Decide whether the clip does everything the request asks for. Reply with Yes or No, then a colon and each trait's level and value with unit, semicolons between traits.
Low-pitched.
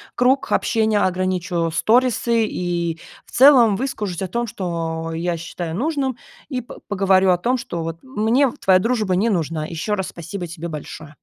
No: high, 190 Hz